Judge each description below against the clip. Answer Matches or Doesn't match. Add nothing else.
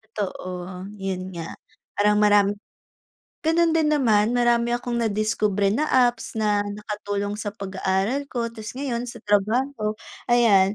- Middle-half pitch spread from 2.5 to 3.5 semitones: Matches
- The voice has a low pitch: Doesn't match